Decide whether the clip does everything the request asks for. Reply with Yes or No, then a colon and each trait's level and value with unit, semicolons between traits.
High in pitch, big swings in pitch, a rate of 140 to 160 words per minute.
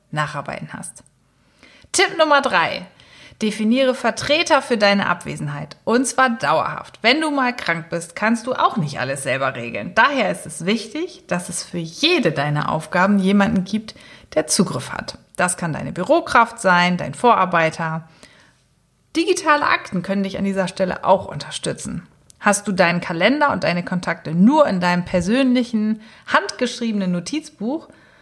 Yes: high, 200 Hz; wide, 6.2 semitones; average, 145 wpm